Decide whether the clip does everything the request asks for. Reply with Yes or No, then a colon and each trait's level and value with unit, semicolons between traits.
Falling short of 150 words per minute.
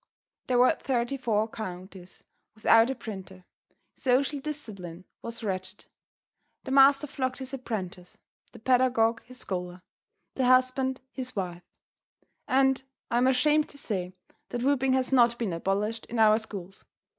Yes: average, 140 wpm